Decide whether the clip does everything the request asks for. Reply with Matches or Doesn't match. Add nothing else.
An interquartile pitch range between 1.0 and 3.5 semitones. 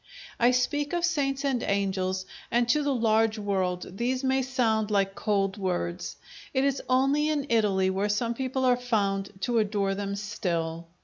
Doesn't match